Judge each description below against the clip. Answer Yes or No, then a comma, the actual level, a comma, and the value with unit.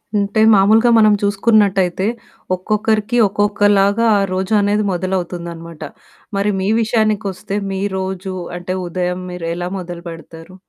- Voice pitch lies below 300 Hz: Yes, high, 195 Hz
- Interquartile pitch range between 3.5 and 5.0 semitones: No, average, 2.7 semitones